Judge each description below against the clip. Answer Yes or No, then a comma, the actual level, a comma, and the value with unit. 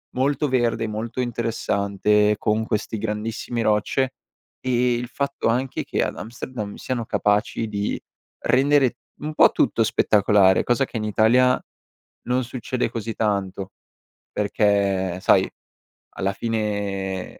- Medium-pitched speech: No, low, 110 Hz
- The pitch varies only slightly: No, average, 3.2 semitones